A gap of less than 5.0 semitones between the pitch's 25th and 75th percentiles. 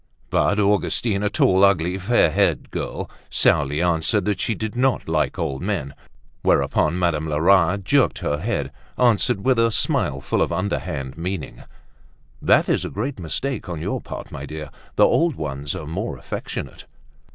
No: average, 5.3 semitones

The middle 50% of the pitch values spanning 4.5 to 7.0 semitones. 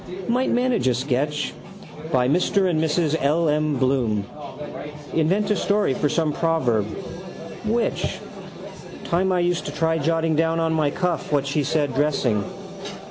No: average, 3.8 semitones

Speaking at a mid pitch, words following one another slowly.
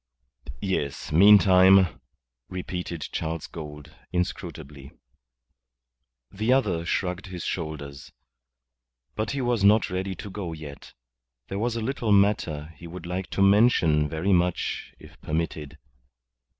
No: very low, 90 Hz; slow, 120 wpm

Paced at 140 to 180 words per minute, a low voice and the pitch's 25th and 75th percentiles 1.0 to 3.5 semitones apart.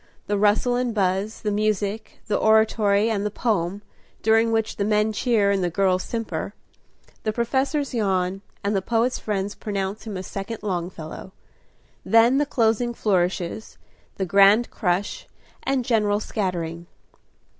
No: average, 145 wpm; high, 210 Hz; narrow, 2.6 semitones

